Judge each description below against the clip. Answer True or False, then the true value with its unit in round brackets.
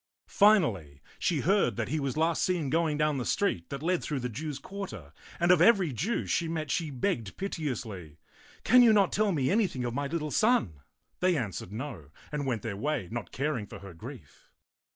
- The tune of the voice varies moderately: False (7.1 semitones)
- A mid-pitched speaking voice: True (150 Hz)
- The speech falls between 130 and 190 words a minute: False (200 wpm)